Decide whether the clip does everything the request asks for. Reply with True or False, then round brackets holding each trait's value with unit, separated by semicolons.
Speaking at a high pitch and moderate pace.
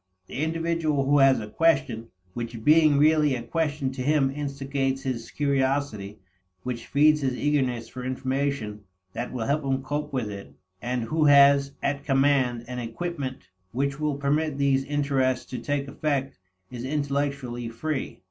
False (135 Hz; 155 wpm)